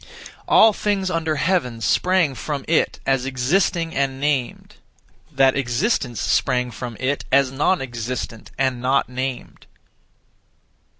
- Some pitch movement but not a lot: Yes, average, 4.2 semitones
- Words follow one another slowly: Yes, slow, 120 wpm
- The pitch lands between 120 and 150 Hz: Yes, low, 135 Hz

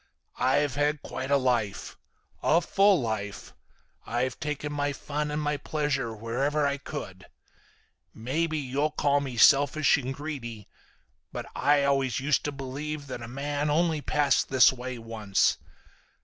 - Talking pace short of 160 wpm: Yes, average, 145 wpm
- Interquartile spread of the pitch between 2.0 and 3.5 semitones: Yes, average, 2.8 semitones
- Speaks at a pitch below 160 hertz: Yes, medium, 140 Hz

